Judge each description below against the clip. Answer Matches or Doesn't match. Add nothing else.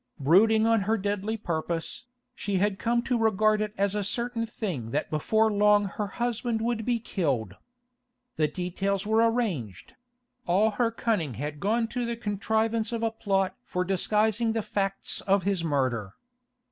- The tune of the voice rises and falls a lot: Doesn't match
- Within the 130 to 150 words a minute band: Doesn't match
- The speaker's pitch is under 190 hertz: Doesn't match